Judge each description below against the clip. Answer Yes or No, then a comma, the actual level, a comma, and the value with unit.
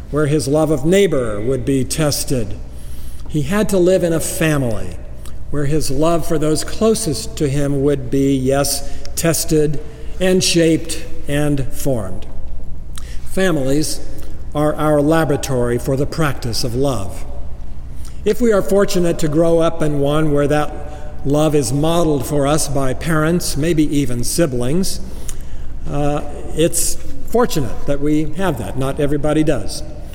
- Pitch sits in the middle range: Yes, medium, 145 Hz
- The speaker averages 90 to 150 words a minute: Yes, average, 140 wpm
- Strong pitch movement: No, average, 4.3 semitones